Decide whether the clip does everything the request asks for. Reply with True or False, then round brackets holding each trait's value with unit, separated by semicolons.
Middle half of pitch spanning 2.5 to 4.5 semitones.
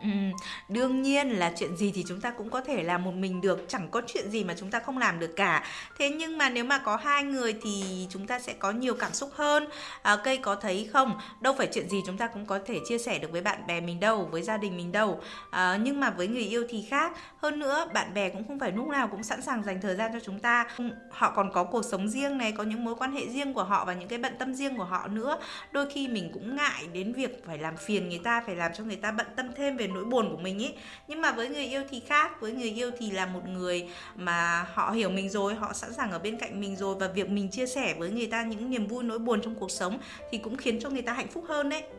False (5.0 semitones)